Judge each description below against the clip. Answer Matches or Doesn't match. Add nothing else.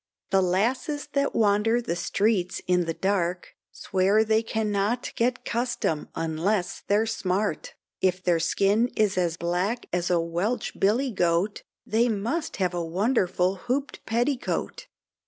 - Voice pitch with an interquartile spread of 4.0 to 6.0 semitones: Matches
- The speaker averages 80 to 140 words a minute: Matches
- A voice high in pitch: Matches